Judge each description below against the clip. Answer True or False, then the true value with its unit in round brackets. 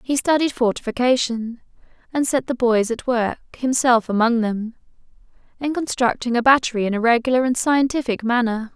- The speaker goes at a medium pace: True (150 wpm)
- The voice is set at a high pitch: True (245 Hz)